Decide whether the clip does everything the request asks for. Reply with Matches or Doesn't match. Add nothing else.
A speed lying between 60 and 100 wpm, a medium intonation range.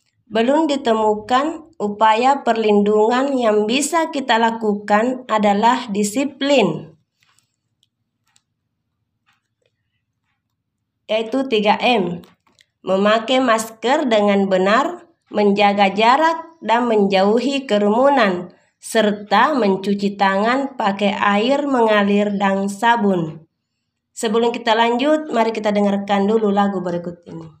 Matches